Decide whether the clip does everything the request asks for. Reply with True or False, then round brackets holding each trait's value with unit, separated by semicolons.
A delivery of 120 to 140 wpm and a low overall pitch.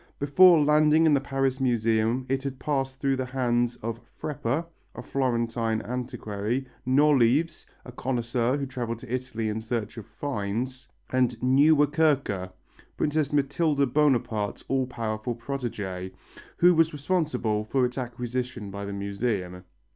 True (135 wpm; 125 Hz)